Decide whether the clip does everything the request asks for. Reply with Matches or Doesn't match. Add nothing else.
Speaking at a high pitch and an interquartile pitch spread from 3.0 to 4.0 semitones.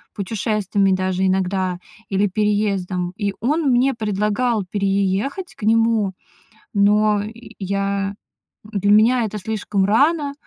Doesn't match